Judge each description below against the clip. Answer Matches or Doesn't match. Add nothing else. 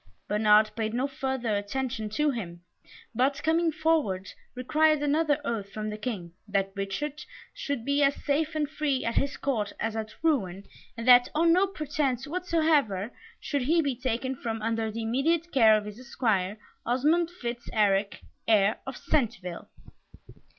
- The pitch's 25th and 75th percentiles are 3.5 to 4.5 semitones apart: Doesn't match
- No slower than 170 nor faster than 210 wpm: Doesn't match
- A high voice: Matches